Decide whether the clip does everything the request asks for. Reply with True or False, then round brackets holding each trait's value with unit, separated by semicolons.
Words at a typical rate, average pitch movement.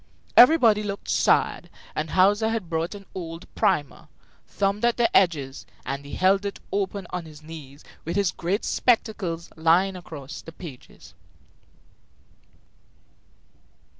False (130 wpm; 3.9 semitones)